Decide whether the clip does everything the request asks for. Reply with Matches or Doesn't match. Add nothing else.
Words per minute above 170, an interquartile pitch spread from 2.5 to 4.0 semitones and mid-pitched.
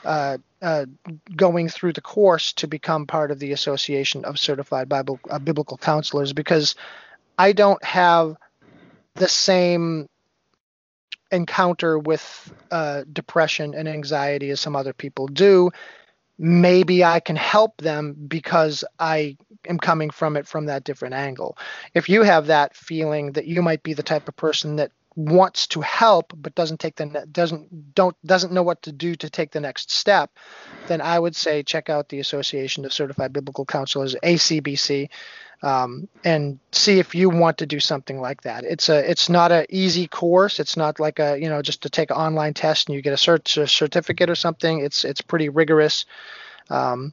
Matches